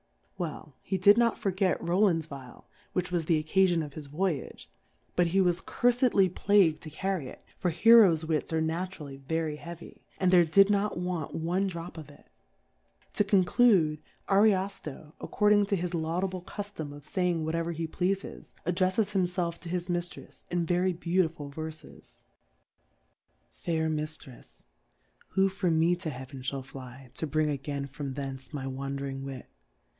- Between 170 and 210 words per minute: No, average, 160 wpm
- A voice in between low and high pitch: Yes, medium, 170 Hz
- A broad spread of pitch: No, average, 3.7 semitones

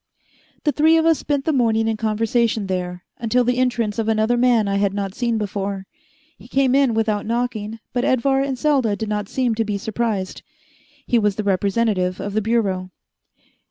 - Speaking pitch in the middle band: No, high, 225 Hz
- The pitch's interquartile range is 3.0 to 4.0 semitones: Yes, average, 3.3 semitones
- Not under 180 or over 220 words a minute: Yes, average, 190 wpm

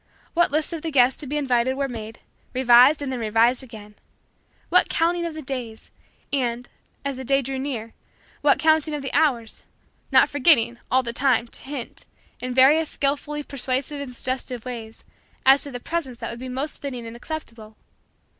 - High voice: Yes, very high, 260 Hz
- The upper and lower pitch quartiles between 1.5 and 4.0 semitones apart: Yes, average, 3.3 semitones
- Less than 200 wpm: Yes, average, 185 wpm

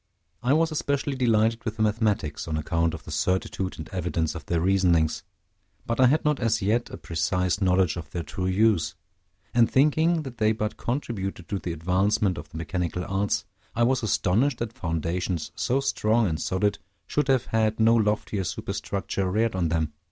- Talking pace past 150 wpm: Yes, average, 180 wpm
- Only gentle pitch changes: No, average, 4.7 semitones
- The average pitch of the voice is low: Yes, low, 100 Hz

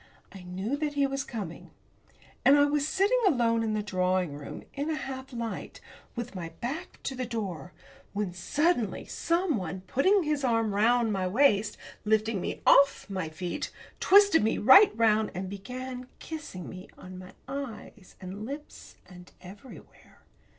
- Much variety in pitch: Yes, wide, 6.7 semitones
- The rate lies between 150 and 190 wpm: Yes, average, 155 wpm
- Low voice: No, high, 225 Hz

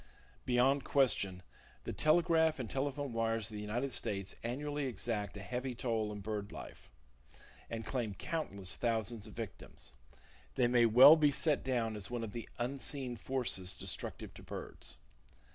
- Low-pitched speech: Yes, low, 120 Hz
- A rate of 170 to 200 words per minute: No, average, 155 wpm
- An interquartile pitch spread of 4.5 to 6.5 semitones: No, average, 4.1 semitones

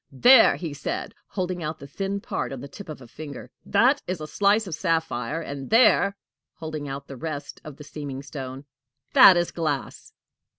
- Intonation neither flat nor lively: Yes, average, 4.8 semitones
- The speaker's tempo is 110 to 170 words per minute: No, average, 185 wpm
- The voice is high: No, medium, 155 Hz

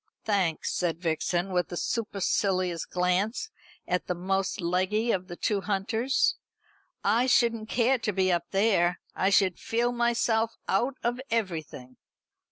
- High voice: Yes, high, 195 Hz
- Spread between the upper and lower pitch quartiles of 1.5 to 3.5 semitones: No, average, 4.1 semitones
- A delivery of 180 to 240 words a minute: No, average, 140 wpm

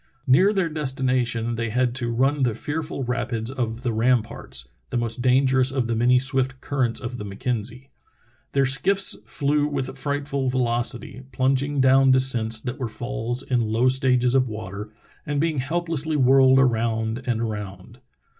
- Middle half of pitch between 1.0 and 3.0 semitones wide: Yes, narrow, 2.5 semitones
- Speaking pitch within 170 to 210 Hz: No, low, 130 Hz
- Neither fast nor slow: Yes, average, 155 wpm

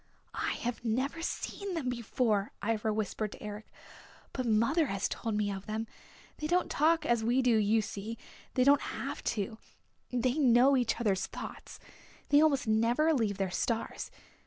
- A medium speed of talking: Yes, average, 165 wpm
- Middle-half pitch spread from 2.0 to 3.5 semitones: No, average, 3.9 semitones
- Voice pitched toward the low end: No, high, 230 Hz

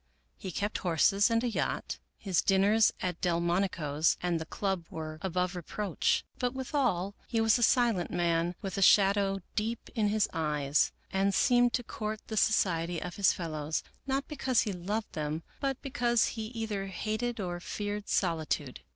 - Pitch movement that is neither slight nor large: Yes, average, 4.4 semitones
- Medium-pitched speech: No, high, 195 Hz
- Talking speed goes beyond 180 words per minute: No, average, 170 wpm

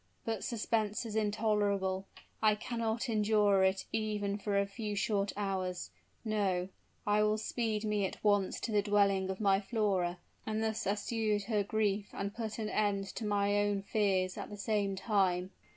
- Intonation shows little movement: Yes, narrow, 1.5 semitones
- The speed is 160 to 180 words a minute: Yes, average, 170 wpm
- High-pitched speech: Yes, high, 205 Hz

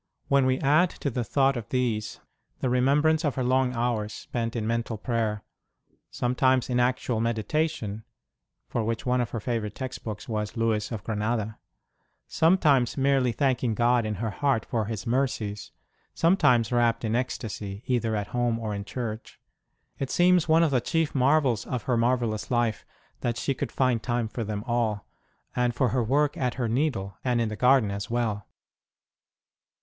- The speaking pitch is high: No, low, 120 Hz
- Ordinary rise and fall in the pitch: Yes, average, 3.0 semitones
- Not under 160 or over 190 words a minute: Yes, average, 175 wpm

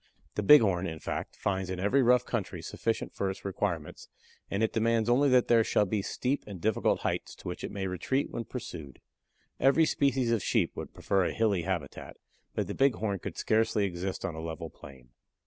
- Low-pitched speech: Yes, low, 100 Hz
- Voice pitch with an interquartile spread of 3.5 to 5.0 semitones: Yes, average, 4.3 semitones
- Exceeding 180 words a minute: Yes, average, 200 wpm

